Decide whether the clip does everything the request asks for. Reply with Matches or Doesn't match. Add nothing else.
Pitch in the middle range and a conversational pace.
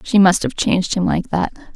Doesn't match